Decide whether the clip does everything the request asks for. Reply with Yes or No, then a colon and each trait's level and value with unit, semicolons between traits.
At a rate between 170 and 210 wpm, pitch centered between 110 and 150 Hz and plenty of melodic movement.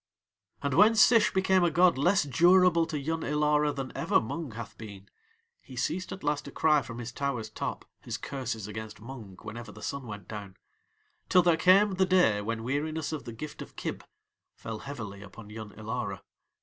Yes: average, 190 wpm; medium, 140 Hz; wide, 6.8 semitones